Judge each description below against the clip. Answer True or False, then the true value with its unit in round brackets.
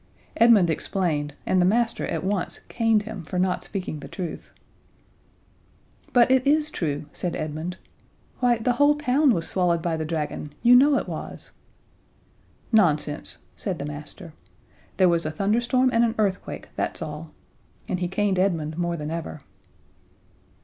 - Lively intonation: True (6.3 semitones)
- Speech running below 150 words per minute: False (155 wpm)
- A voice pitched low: False (185 Hz)